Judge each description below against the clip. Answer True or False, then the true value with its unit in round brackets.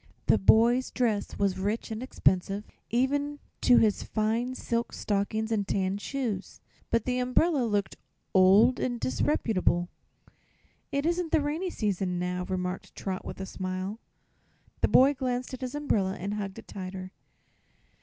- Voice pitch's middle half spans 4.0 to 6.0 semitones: True (5.0 semitones)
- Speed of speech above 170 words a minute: False (145 wpm)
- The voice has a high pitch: True (220 Hz)